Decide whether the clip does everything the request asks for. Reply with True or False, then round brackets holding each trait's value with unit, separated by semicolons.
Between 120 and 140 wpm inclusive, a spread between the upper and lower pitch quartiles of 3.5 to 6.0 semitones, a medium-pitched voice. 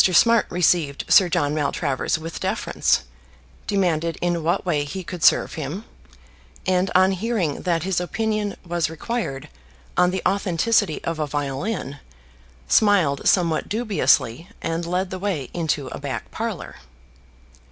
True (135 wpm; 3.8 semitones; 175 Hz)